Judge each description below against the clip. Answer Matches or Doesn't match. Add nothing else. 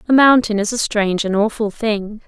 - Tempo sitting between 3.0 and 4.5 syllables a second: Doesn't match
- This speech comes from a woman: Matches